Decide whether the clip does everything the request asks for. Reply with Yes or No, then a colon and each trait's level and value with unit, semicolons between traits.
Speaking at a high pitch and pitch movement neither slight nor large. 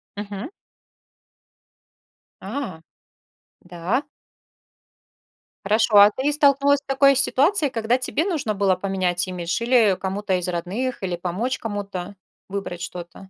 No: high, 205 Hz; wide, 6.0 semitones